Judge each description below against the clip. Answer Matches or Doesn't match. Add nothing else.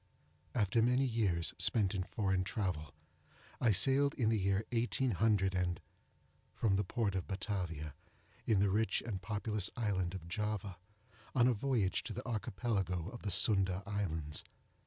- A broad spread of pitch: Doesn't match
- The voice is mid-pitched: Doesn't match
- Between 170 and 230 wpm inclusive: Doesn't match